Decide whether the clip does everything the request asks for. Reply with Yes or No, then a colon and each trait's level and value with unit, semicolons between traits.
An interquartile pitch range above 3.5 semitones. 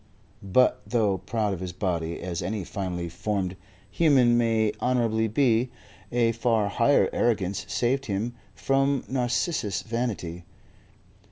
Yes: average, 4.1 semitones